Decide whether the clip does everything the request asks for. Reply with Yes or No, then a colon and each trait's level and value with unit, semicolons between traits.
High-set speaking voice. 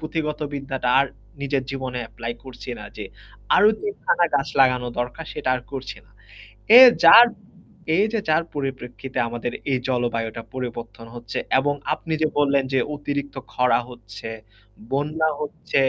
No: low, 135 Hz